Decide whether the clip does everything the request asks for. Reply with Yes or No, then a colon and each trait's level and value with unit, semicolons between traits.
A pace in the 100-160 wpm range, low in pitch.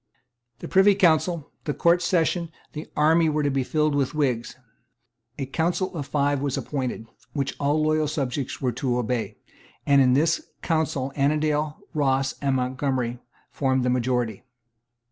No: average, 155 wpm; medium, 145 Hz